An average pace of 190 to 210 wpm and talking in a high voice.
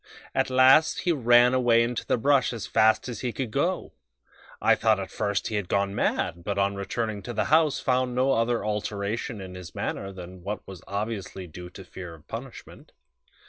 No: average, 200 wpm; low, 110 Hz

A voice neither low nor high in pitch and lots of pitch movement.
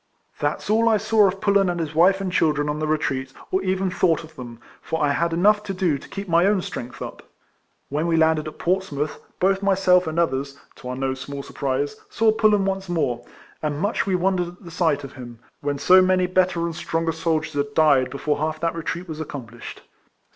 No: medium, 165 Hz; average, 4.4 semitones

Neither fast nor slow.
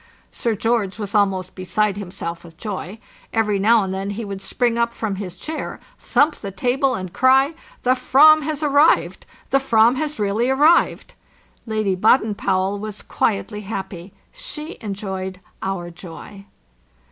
Yes: average, 150 wpm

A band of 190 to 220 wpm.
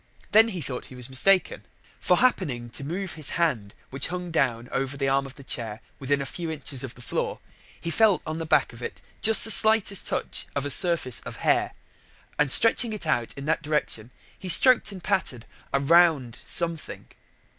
Yes: average, 200 wpm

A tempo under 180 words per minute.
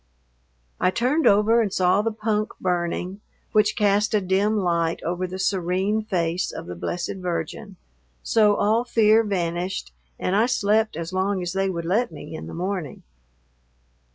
Yes: average, 160 wpm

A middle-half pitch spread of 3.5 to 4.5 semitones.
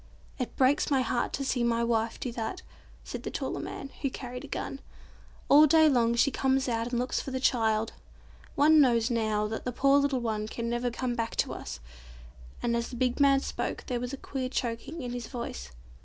No: narrow, 2.6 semitones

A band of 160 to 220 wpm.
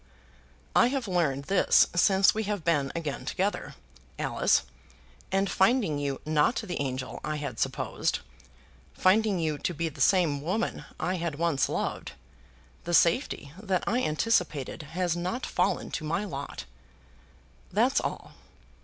No: average, 140 wpm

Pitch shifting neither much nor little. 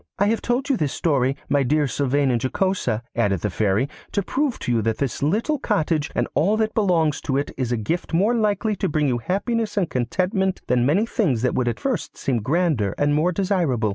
No: wide, 8.0 semitones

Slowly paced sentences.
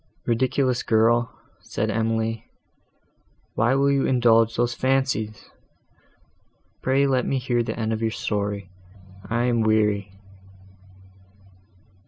Yes: slow, 110 wpm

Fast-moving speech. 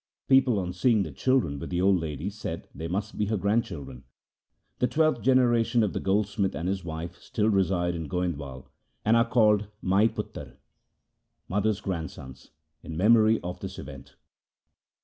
No: average, 160 wpm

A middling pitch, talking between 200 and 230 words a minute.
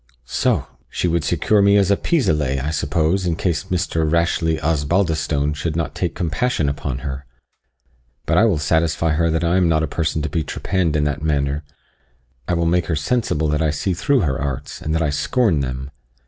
No: very low, 80 Hz; fast, 205 wpm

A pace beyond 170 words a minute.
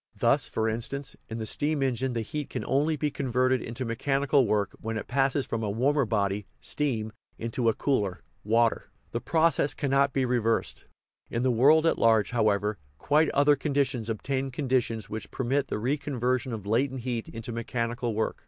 Yes: average, 180 wpm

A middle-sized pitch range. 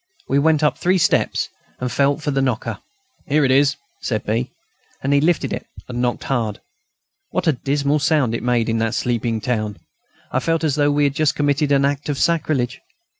Yes: average, 3.3 semitones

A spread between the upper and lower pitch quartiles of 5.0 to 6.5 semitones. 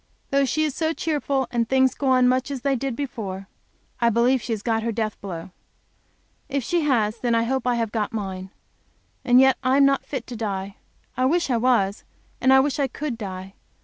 No: average, 3.5 semitones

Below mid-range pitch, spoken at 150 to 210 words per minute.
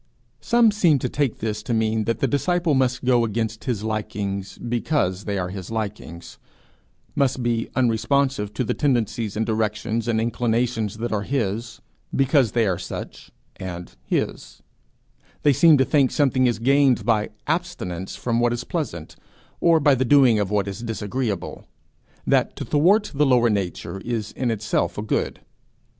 Yes: low, 115 Hz; average, 165 wpm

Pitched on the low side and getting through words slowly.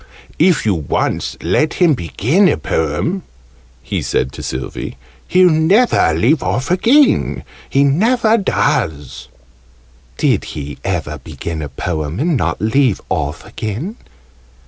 Yes: low, 120 Hz; slow, 125 wpm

